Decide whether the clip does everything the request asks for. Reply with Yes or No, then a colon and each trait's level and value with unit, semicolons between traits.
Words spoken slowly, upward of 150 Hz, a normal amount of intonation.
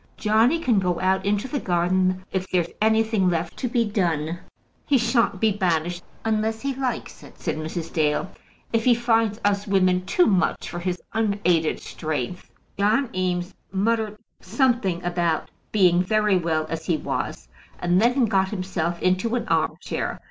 No: average, 165 wpm; high, 190 Hz; average, 4.1 semitones